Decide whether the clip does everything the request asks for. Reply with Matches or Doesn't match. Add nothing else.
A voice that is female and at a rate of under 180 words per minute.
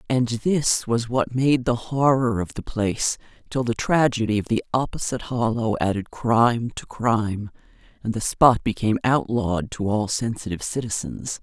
Matches